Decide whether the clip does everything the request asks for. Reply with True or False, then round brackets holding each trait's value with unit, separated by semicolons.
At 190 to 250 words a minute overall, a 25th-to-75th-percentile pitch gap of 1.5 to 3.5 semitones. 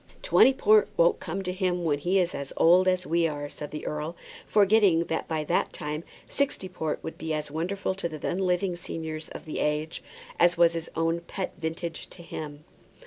True (200 wpm; 2.8 semitones)